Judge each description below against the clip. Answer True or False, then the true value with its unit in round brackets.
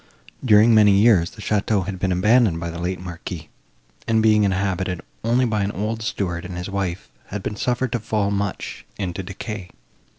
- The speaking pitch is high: False (100 Hz)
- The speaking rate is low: False (185 wpm)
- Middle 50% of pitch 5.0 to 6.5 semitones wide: False (3.1 semitones)